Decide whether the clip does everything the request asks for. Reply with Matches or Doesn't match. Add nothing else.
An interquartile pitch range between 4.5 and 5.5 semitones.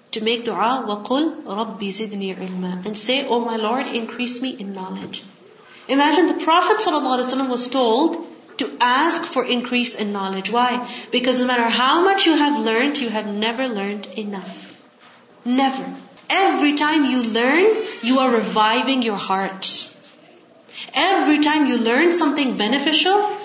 Matches